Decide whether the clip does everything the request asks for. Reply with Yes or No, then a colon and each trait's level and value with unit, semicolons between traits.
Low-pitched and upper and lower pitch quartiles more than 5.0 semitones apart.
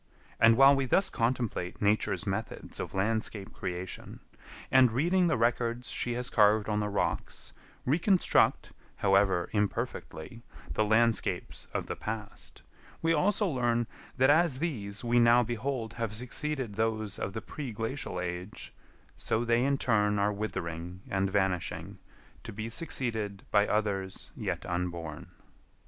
No: low, 110 Hz; average, 3.7 semitones